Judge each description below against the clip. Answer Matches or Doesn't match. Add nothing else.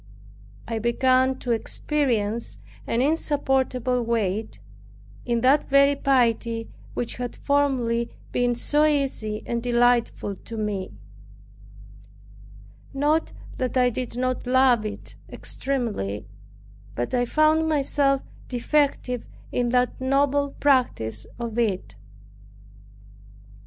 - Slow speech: Matches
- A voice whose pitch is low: Doesn't match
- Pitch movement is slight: Doesn't match